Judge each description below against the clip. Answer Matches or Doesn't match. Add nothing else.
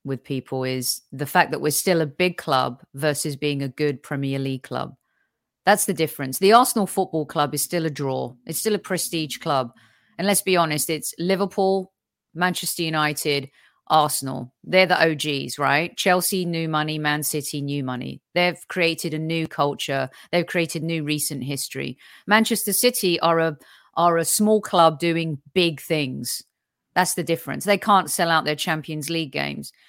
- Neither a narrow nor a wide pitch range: Matches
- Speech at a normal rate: Matches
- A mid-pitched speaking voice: Matches